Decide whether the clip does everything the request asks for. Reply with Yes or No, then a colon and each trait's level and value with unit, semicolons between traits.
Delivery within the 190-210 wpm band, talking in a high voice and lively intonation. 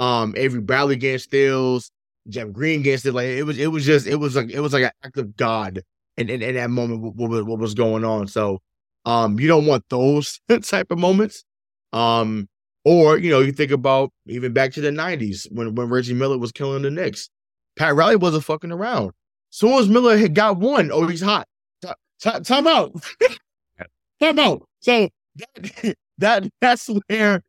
No: average, 200 wpm; low, 135 Hz; wide, 6.8 semitones